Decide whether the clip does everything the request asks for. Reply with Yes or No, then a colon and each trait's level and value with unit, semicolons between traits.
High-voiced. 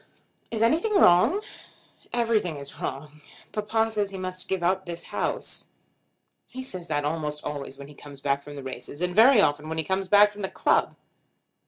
No: medium, 180 Hz